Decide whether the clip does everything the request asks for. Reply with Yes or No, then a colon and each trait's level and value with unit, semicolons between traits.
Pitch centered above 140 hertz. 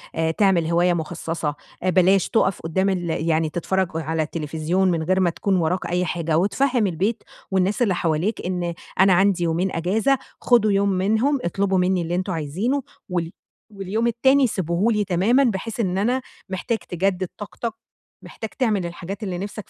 Yes: medium, 185 Hz